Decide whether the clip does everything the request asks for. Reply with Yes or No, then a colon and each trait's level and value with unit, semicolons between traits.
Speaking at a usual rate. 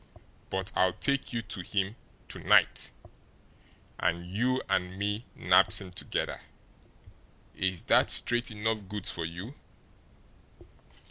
No: slow, 120 wpm